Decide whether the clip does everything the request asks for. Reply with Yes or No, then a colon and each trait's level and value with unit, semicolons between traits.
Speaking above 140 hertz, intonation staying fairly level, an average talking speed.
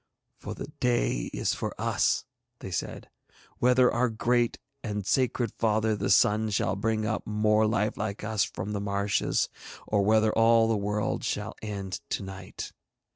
No: low, 105 Hz; narrow, 1.7 semitones; average, 160 wpm